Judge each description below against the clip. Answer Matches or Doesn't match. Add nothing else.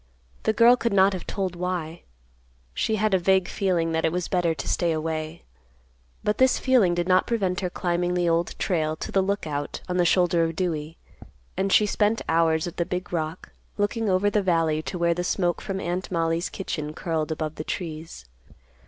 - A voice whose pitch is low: Doesn't match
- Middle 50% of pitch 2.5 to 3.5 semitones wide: Matches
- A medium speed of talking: Matches